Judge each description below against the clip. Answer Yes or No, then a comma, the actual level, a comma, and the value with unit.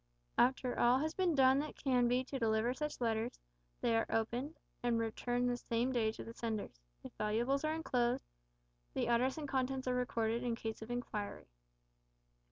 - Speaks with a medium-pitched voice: No, high, 245 Hz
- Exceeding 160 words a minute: Yes, average, 175 wpm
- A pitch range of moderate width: No, narrow, 2.3 semitones